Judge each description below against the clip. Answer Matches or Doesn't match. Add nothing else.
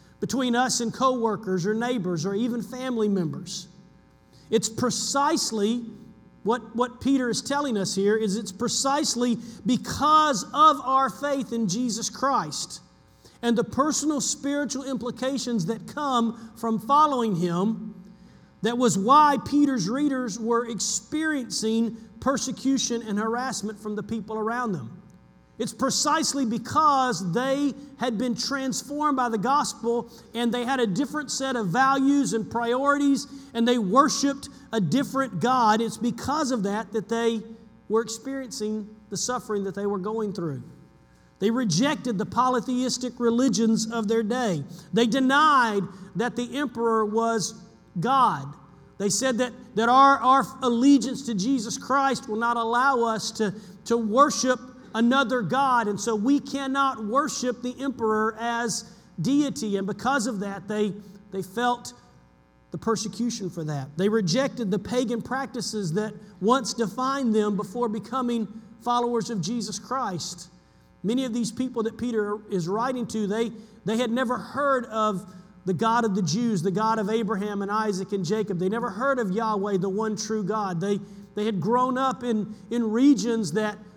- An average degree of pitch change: Matches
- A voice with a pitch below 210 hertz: Doesn't match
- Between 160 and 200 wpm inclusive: Doesn't match